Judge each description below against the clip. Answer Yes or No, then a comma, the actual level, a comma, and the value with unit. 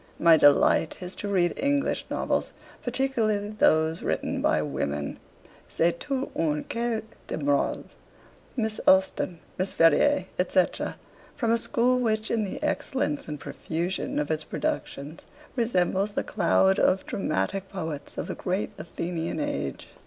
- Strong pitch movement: Yes, wide, 6.0 semitones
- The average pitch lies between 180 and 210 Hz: Yes, high, 190 Hz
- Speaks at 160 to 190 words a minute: No, average, 140 wpm